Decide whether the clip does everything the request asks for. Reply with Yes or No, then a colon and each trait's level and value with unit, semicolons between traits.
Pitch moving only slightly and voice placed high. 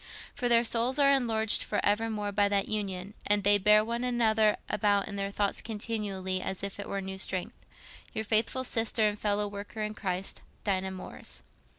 Yes: narrow, 2.0 semitones; high, 210 Hz